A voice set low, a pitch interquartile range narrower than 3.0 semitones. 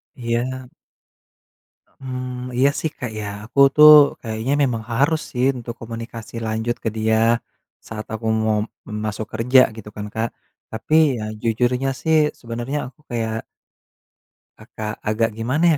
Yes: low, 115 Hz; narrow, 2.5 semitones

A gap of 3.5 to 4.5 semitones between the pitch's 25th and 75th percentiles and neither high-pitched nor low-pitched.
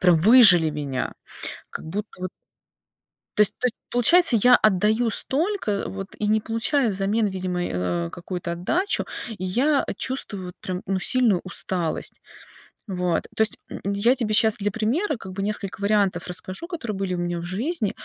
No: average, 4.2 semitones; high, 200 Hz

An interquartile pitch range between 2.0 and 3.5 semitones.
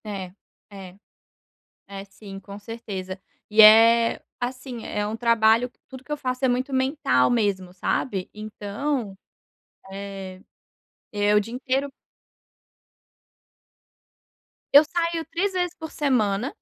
No: average, 4.6 semitones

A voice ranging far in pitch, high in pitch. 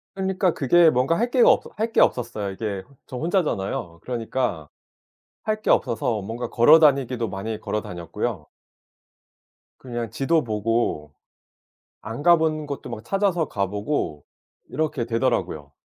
No: wide, 7.0 semitones; low, 120 Hz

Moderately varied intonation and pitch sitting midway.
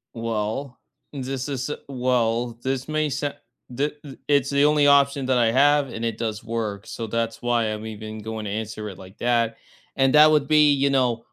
No: average, 3.9 semitones; low, 125 Hz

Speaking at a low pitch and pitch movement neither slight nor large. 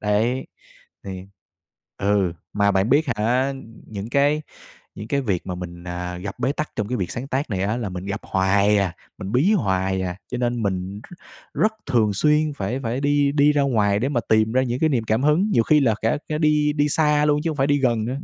No: low, 120 Hz; wide, 6.3 semitones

